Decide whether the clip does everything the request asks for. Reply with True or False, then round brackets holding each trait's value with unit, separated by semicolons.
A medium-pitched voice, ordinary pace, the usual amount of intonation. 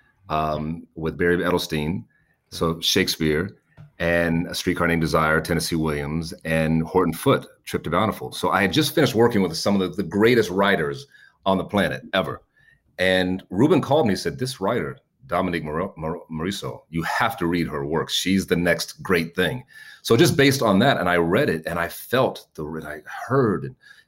False (85 Hz; 185 wpm; 3.2 semitones)